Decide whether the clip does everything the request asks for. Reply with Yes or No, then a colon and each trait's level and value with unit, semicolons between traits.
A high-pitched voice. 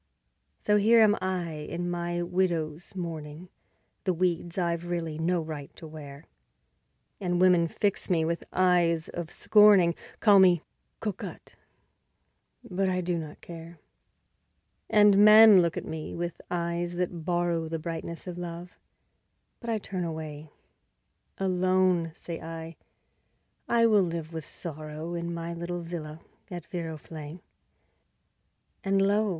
No: medium, 175 Hz